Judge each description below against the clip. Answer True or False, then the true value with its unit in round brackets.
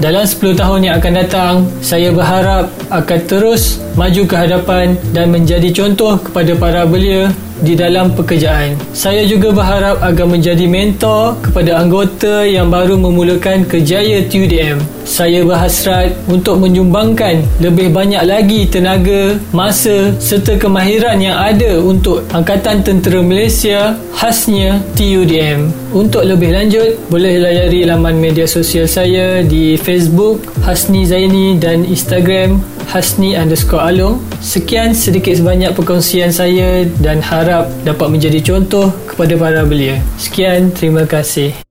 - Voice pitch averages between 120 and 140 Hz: False (180 Hz)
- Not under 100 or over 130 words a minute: True (125 wpm)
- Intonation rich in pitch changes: False (2.5 semitones)